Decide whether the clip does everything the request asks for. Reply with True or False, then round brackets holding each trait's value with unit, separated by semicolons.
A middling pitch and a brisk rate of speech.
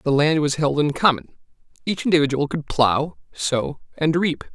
False (150 Hz; 170 wpm)